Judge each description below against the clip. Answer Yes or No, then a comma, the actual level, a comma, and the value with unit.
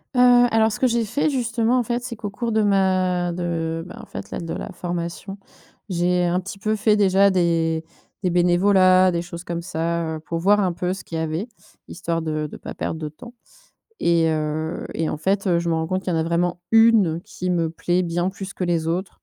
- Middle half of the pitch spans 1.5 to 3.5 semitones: Yes, average, 3.1 semitones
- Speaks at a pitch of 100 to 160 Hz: No, medium, 180 Hz